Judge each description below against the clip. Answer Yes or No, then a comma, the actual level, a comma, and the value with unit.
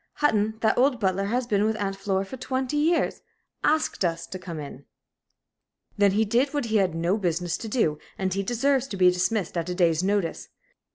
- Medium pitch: No, high, 200 Hz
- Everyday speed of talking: No, fast, 210 wpm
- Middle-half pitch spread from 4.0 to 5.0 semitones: Yes, average, 4.7 semitones